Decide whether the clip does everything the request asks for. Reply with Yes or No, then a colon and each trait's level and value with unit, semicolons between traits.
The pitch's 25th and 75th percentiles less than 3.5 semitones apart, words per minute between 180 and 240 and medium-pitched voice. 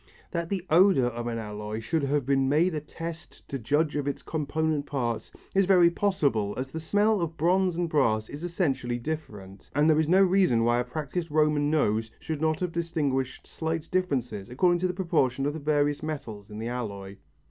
No: wide, 5.4 semitones; average, 200 wpm; medium, 150 Hz